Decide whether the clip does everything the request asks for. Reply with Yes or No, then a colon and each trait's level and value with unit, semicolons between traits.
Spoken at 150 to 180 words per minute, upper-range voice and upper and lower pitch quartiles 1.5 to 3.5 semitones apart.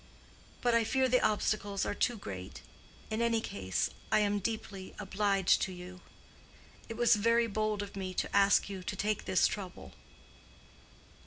Yes: average, 160 wpm; high, 205 Hz; average, 2.8 semitones